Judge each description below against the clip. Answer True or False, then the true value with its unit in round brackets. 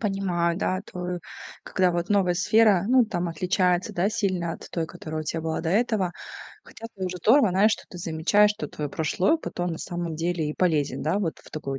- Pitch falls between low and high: True (180 Hz)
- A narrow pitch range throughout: False (3.1 semitones)